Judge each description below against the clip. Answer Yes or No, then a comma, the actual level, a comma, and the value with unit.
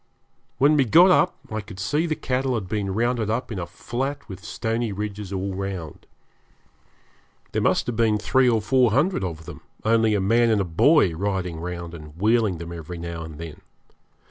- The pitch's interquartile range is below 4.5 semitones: No, average, 5.1 semitones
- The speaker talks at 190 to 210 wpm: Yes, average, 195 wpm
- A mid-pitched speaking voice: No, low, 105 Hz